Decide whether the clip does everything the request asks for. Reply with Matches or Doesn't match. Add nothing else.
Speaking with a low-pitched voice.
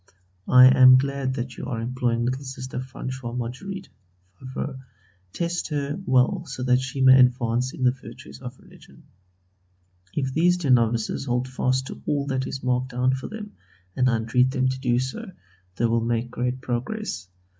Matches